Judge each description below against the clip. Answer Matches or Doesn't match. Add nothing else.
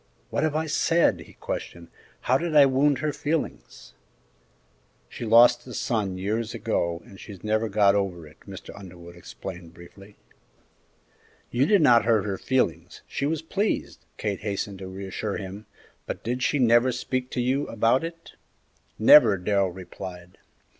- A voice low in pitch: Matches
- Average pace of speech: Matches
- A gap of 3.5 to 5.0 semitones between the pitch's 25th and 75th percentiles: Doesn't match